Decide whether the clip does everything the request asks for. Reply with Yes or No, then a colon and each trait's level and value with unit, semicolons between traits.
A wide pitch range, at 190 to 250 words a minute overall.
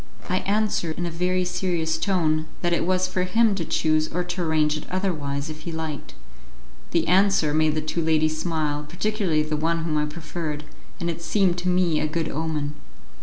No: average, 2.7 semitones; average, 195 wpm